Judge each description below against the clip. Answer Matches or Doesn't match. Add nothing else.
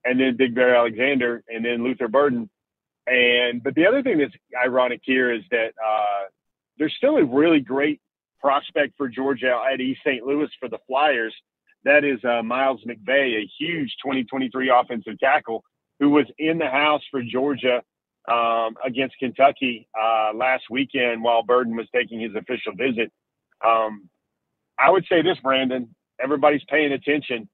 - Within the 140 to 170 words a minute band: Matches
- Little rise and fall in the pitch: Doesn't match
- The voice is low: Matches